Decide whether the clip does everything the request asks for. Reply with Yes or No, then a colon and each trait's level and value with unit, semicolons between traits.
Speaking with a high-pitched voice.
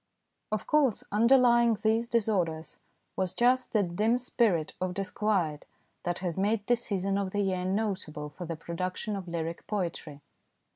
Yes: high, 195 Hz